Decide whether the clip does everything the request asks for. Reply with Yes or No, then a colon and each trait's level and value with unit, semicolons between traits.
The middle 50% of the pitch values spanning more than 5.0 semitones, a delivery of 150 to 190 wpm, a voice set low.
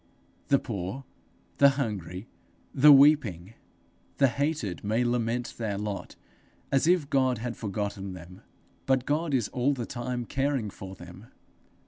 No: wide, 5.4 semitones; slow, 135 wpm; low, 120 Hz